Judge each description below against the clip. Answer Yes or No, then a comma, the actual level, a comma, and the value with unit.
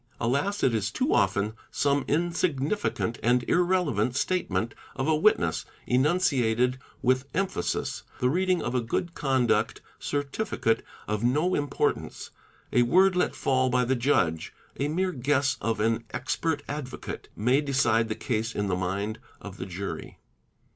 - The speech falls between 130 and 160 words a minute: Yes, average, 145 wpm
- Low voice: Yes, low, 130 Hz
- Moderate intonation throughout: Yes, average, 5.0 semitones